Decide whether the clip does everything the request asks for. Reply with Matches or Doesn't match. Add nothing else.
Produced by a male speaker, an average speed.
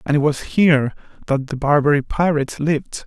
Matches